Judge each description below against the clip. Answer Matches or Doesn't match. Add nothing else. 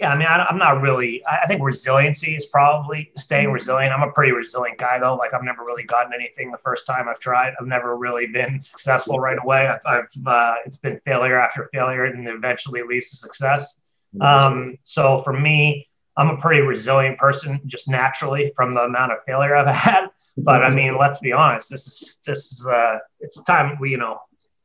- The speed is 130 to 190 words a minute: Doesn't match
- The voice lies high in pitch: Doesn't match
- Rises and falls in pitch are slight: Matches